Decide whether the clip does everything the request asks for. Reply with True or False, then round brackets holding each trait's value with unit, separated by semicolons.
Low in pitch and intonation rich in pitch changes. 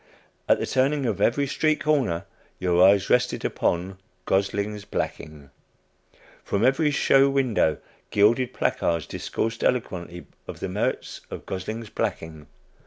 True (105 Hz; 6.3 semitones)